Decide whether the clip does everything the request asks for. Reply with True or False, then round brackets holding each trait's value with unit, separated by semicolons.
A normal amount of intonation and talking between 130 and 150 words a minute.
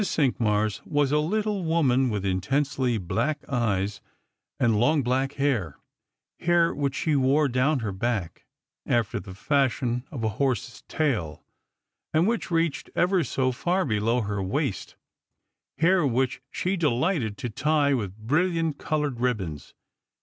False (5.7 semitones; 140 wpm)